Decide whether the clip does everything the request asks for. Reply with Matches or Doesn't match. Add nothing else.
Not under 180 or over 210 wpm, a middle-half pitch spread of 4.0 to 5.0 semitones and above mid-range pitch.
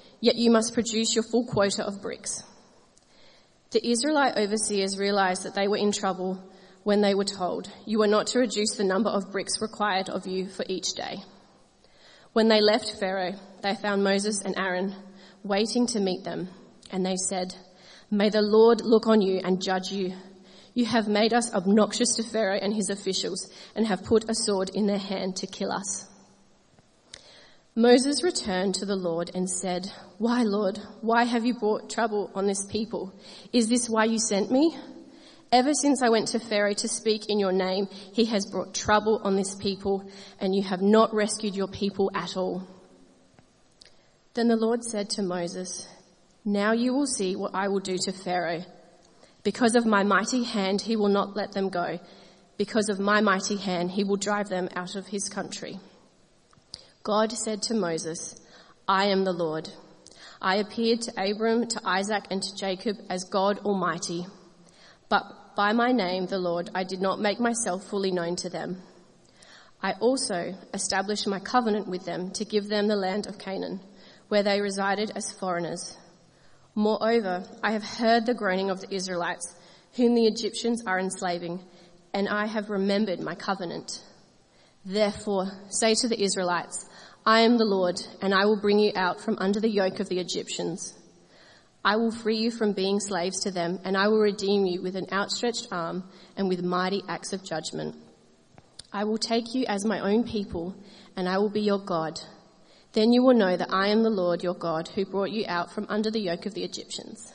Doesn't match